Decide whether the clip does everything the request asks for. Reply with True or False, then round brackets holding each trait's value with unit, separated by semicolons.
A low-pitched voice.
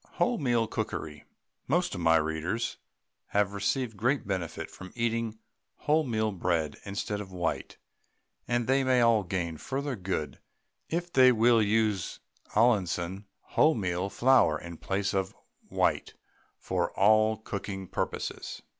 True (105 Hz)